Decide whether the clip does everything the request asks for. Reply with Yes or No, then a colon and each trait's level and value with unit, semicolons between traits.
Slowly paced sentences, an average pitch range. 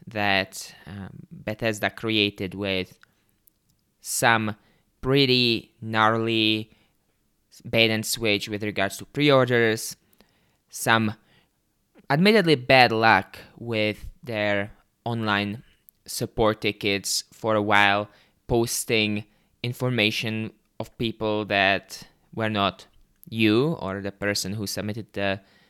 No: slow, 100 wpm; narrow, 2.0 semitones